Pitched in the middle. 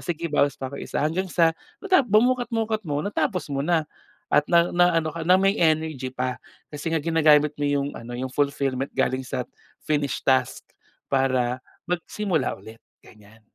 Yes: medium, 150 Hz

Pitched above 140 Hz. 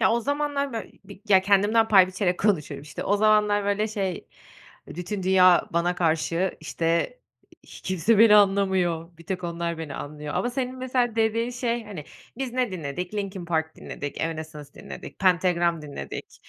Yes: high, 190 Hz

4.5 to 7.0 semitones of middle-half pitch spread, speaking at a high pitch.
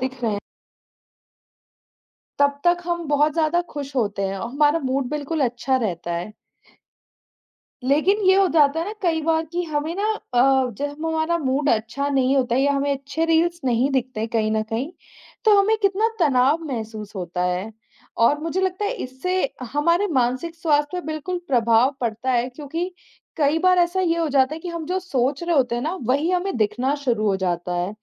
Yes: wide, 5.4 semitones; very high, 285 Hz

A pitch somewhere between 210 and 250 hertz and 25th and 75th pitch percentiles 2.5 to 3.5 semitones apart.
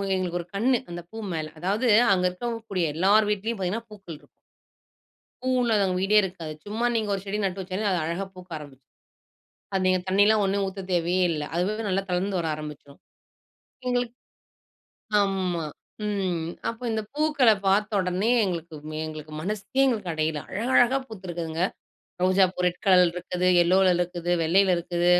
No: medium, 185 Hz; average, 3.2 semitones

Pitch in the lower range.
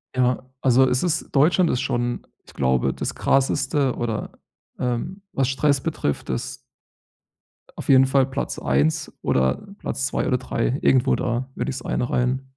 Yes: low, 130 Hz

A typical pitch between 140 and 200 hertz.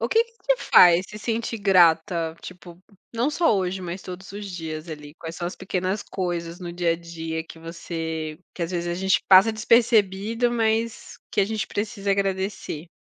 Yes: medium, 185 Hz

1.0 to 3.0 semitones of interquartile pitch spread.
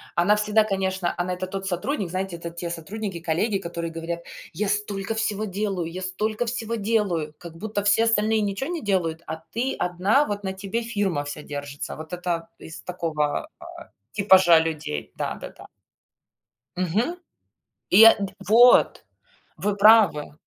No: average, 4.0 semitones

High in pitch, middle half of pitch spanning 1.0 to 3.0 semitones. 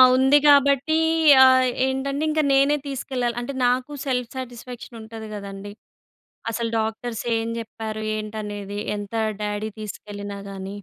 No: high, 230 Hz; average, 3.9 semitones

